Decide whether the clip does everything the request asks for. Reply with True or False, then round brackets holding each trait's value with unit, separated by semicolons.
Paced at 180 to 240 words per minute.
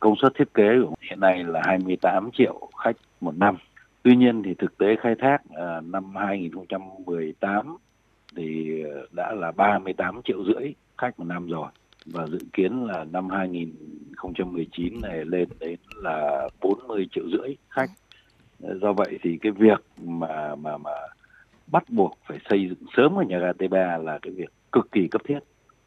False (165 wpm)